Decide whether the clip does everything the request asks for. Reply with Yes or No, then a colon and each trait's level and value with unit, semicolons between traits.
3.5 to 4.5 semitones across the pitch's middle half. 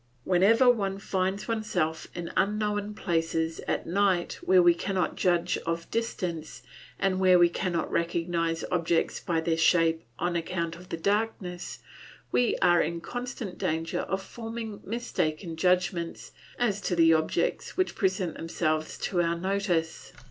No: average, 3.1 semitones